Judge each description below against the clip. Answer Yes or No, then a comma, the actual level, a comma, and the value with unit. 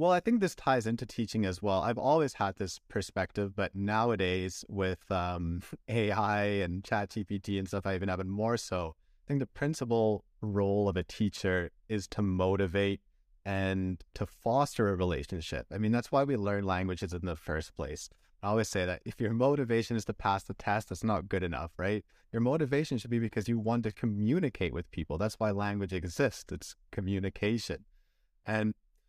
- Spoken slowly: No, average, 190 wpm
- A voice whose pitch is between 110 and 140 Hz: No, low, 100 Hz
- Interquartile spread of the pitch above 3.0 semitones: Yes, average, 3.4 semitones